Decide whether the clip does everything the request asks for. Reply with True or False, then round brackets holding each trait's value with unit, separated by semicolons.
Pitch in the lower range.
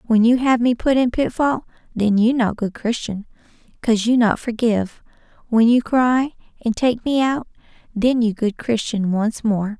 False (230 Hz)